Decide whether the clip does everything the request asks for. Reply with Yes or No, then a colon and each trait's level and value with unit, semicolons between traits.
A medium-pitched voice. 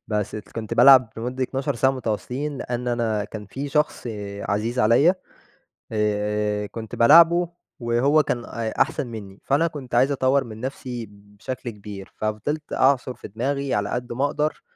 No: low, 120 Hz